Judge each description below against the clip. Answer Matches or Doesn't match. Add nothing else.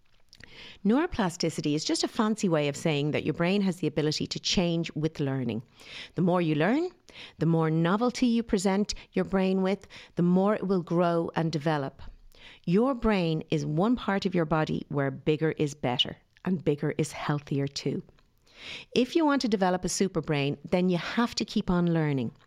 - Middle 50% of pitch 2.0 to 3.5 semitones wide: Doesn't match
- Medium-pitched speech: Matches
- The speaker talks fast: Doesn't match